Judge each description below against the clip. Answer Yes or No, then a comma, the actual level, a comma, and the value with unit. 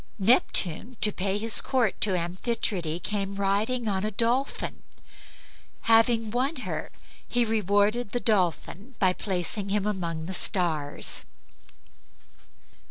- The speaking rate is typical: No, slow, 115 wpm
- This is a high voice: Yes, high, 205 Hz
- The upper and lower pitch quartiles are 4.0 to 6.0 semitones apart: No, average, 3.6 semitones